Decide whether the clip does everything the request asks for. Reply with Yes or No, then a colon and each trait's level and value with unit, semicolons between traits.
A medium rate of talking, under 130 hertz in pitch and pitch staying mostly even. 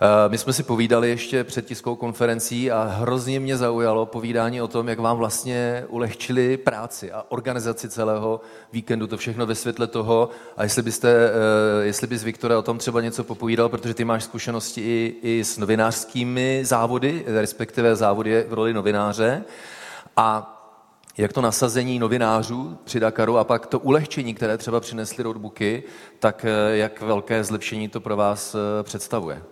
Yes: average, 155 wpm; low, 115 Hz; narrow, 1.5 semitones